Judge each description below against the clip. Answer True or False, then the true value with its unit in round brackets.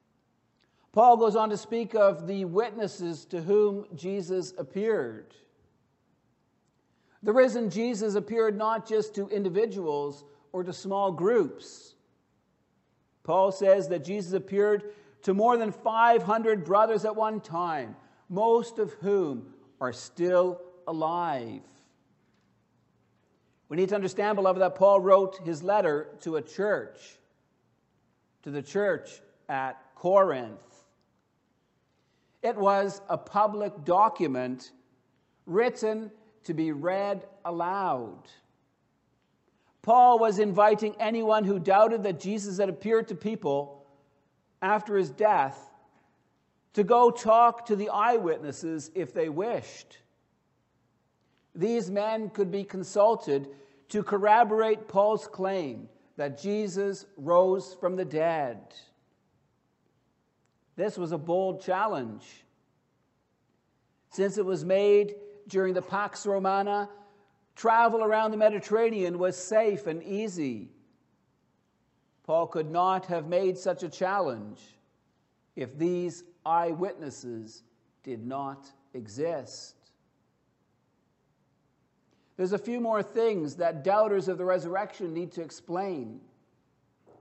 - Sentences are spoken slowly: True (110 wpm)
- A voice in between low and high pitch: False (195 Hz)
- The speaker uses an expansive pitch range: False (3.8 semitones)